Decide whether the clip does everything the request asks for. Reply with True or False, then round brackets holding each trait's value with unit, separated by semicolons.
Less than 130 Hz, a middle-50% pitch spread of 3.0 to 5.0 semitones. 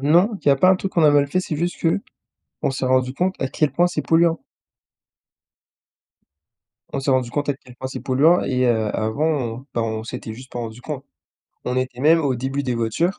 False (135 Hz; 4.3 semitones)